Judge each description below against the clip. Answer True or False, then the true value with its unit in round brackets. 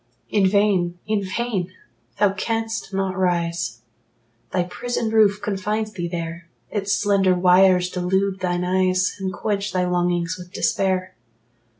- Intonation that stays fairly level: True (2.2 semitones)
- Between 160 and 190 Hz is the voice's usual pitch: True (185 Hz)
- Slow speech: True (130 wpm)